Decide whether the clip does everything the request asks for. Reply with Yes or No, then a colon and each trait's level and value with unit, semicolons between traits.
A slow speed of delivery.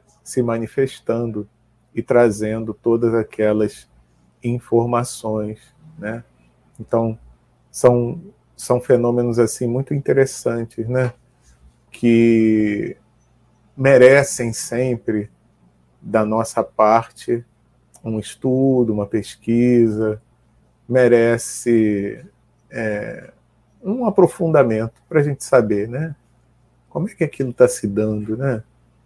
Yes: slow, 90 wpm